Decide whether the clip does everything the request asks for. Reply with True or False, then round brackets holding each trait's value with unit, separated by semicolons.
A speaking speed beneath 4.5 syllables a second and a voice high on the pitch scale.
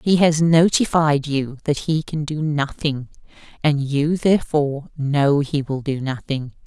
False (4.2 syllables/s; 150 Hz)